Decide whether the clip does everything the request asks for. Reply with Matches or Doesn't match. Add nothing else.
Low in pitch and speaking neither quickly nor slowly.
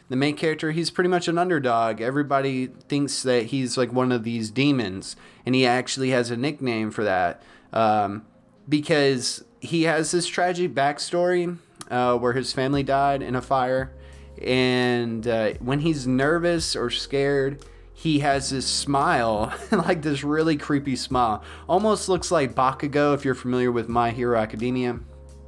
Matches